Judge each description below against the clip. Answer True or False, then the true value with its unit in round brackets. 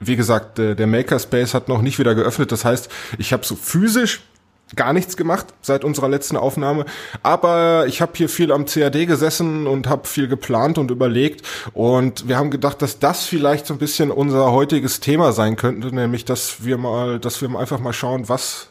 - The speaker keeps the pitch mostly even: False (3.5 semitones)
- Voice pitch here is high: False (135 Hz)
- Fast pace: True (195 wpm)